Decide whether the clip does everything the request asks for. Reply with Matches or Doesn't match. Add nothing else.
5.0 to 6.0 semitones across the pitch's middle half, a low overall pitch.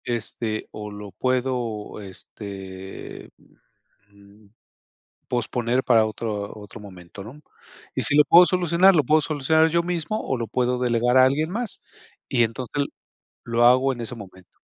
Matches